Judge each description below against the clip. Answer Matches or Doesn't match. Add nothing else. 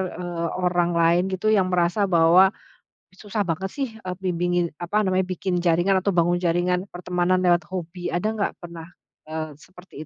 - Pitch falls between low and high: Matches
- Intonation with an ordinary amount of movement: Doesn't match